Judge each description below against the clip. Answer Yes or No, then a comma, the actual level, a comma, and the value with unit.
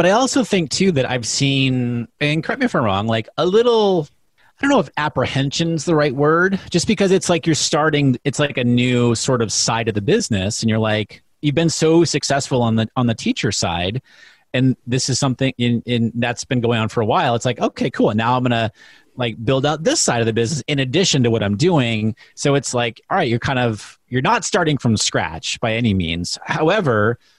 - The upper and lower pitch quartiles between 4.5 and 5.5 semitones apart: Yes, average, 5.2 semitones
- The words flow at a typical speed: No, fast, 260 wpm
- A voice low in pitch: Yes, low, 130 Hz